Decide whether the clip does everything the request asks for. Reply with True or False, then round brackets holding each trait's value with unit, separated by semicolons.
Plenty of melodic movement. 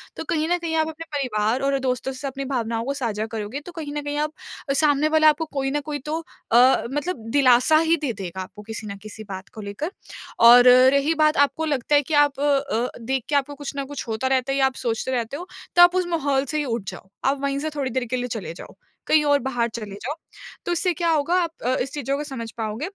False (4.0 semitones)